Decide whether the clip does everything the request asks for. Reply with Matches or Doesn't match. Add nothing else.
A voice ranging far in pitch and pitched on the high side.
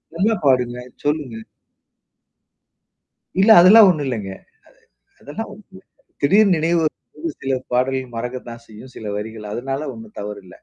Doesn't match